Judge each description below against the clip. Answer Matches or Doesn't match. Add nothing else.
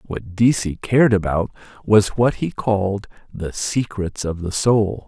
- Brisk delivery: Doesn't match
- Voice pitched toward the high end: Doesn't match